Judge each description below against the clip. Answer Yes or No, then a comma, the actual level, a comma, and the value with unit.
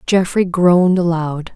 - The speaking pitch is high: No, medium, 175 Hz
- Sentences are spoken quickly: No, slow, 115 wpm